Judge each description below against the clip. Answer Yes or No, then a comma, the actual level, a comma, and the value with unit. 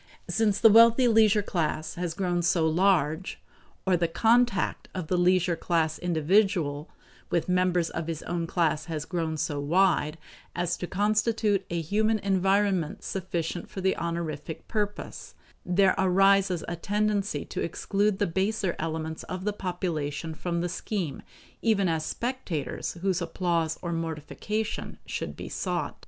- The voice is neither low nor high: Yes, medium, 180 Hz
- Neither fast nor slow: Yes, average, 145 wpm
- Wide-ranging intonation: No, average, 3.4 semitones